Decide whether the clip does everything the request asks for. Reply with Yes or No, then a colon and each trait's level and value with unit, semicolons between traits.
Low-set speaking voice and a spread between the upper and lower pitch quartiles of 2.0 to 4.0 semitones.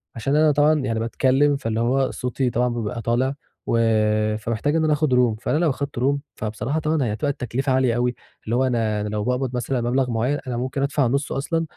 Yes: low, 130 Hz; average, 3.2 semitones